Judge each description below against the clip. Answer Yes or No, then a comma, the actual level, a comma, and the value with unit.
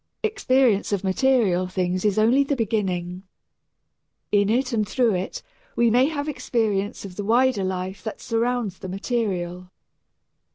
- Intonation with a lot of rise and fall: No, average, 4.7 semitones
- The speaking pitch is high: Yes, high, 210 Hz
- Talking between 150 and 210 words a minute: No, average, 140 wpm